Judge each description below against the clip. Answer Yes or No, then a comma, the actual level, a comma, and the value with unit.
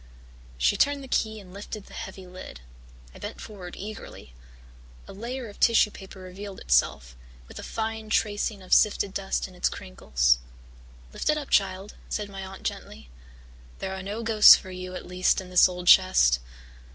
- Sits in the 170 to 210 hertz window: Yes, high, 190 Hz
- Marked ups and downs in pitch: No, average, 2.7 semitones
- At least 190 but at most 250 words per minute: No, average, 175 wpm